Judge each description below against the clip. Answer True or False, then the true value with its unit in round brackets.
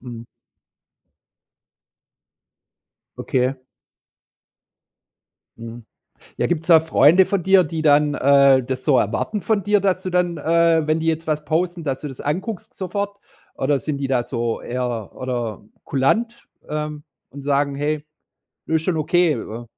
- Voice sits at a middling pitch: True (150 Hz)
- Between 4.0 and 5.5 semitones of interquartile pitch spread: True (4.7 semitones)